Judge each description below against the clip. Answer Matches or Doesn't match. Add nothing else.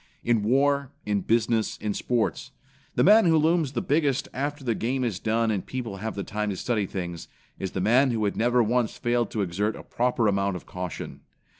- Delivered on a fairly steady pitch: Doesn't match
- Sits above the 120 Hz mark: Doesn't match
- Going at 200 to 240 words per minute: Matches